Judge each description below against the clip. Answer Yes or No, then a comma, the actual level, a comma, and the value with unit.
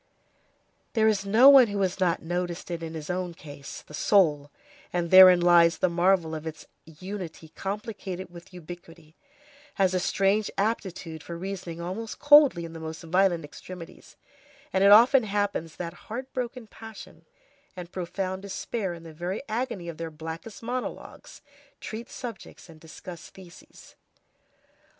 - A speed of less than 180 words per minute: Yes, average, 145 wpm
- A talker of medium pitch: Yes, medium, 180 Hz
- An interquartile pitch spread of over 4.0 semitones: No, average, 3.5 semitones